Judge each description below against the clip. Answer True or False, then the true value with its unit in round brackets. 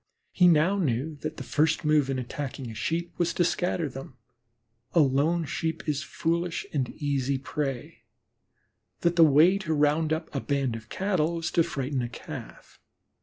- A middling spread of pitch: True (3.5 semitones)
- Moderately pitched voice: True (150 Hz)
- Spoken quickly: False (170 wpm)